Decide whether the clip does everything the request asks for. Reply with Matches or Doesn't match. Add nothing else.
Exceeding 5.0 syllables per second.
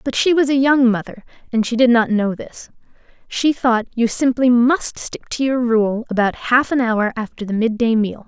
Doesn't match